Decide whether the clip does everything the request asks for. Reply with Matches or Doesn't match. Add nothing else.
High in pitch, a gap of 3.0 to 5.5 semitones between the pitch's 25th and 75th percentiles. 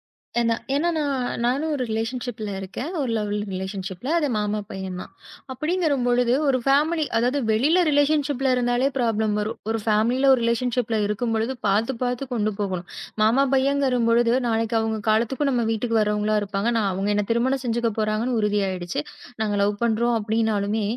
Matches